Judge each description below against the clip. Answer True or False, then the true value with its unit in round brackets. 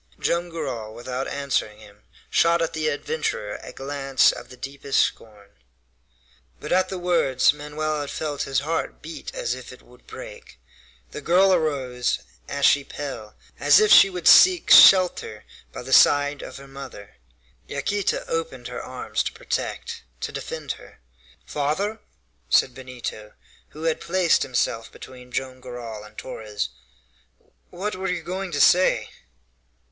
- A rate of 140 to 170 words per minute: True (150 wpm)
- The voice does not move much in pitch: False (5.3 semitones)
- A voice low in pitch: False (145 Hz)